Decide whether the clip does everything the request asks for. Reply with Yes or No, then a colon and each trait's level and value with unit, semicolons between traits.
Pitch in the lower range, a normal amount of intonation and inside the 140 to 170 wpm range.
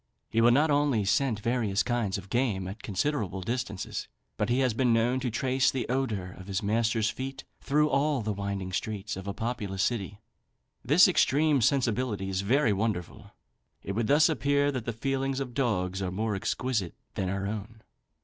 No: low, 115 Hz; average, 4.9 semitones; average, 180 wpm